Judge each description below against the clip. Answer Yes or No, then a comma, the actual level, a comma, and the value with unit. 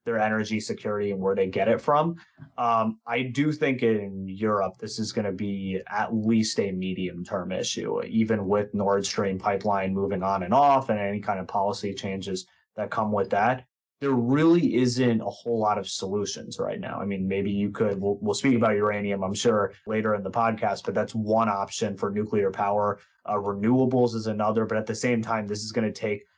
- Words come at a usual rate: No, fast, 210 wpm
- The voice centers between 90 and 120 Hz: Yes, low, 105 Hz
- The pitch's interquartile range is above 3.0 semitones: No, narrow, 2.4 semitones